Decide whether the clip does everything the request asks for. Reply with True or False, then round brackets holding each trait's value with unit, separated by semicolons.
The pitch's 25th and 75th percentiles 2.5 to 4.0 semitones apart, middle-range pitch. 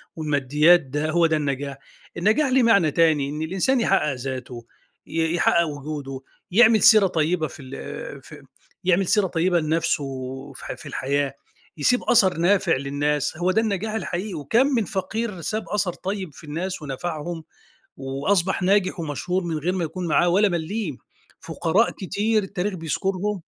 False (4.8 semitones; 175 Hz)